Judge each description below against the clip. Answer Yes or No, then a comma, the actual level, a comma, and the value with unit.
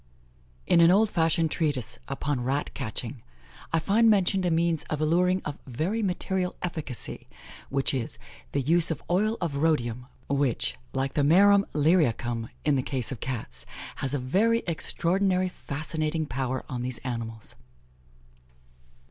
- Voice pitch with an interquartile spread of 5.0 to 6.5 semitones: Yes, wide, 5.5 semitones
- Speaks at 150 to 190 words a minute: No, average, 140 wpm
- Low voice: No, medium, 155 Hz